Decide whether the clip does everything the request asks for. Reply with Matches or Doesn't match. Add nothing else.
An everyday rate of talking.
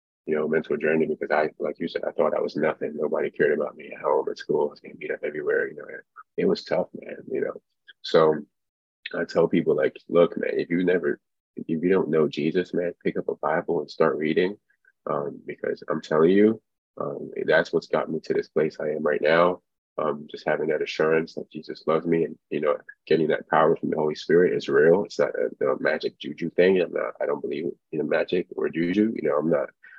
Doesn't match